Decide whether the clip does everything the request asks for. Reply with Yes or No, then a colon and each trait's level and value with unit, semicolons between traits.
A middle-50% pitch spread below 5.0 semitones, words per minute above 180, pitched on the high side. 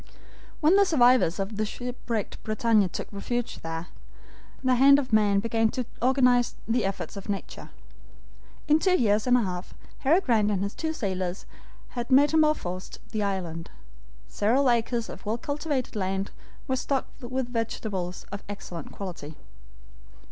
No: average, 4.5 semitones; average, 150 wpm; high, 225 Hz